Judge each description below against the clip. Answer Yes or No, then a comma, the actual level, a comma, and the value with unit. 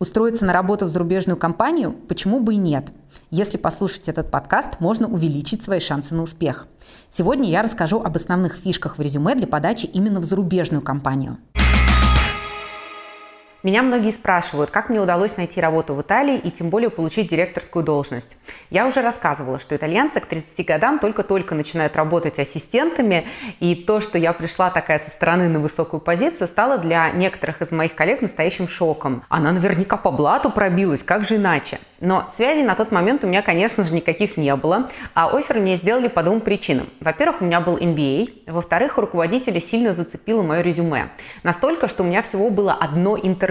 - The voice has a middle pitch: Yes, medium, 180 Hz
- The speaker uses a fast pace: Yes, fast, 175 wpm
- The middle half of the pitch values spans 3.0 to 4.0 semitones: No, average, 4.5 semitones